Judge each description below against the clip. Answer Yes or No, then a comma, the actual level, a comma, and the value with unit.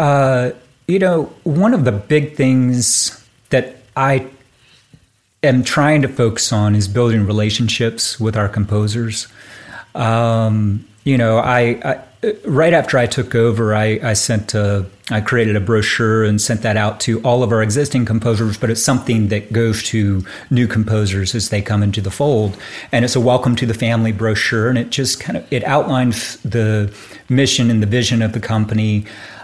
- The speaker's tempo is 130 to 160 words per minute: No, average, 175 wpm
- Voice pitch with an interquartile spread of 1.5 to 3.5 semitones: Yes, average, 2.8 semitones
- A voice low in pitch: Yes, low, 115 Hz